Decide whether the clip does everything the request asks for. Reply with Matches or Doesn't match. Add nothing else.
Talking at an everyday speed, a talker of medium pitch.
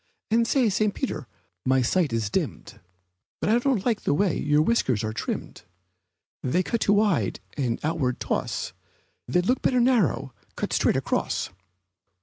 Matches